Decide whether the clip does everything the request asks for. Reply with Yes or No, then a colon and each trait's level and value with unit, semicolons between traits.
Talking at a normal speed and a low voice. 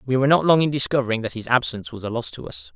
No: fast, 305 wpm; low, 125 Hz